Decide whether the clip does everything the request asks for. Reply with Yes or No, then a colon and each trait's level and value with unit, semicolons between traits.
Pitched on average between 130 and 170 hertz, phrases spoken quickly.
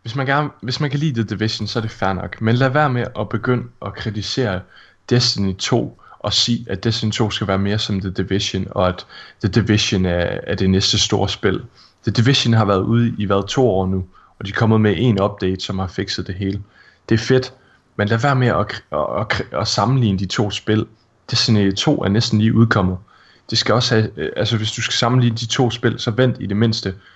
No: low, 110 Hz; fast, 235 wpm